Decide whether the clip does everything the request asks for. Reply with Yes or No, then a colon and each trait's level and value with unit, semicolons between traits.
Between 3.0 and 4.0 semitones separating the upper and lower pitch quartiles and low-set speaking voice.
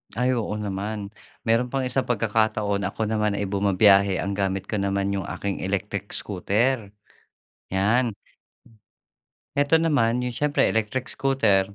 Yes: average, 3.5 semitones; low, 105 Hz